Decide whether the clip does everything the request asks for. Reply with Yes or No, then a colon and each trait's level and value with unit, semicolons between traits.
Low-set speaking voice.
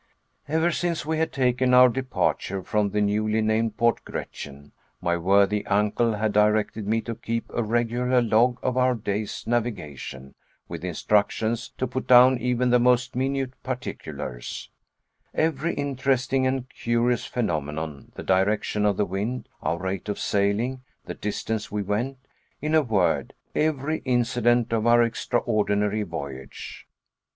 Yes: low, 115 Hz